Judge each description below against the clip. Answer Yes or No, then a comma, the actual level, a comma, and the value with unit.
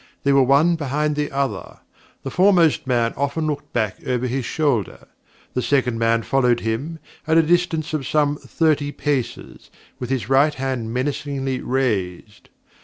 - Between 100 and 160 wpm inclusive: Yes, average, 155 wpm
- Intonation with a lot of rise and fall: No, average, 3.4 semitones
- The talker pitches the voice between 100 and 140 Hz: Yes, low, 135 Hz